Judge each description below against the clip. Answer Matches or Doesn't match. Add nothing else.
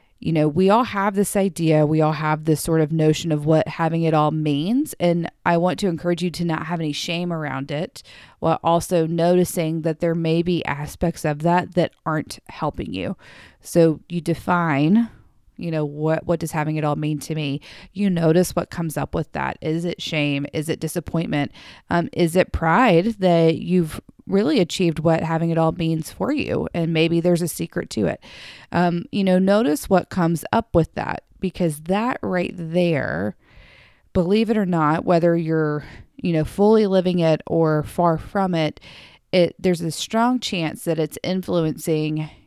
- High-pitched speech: Doesn't match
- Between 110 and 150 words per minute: Doesn't match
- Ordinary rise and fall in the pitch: Doesn't match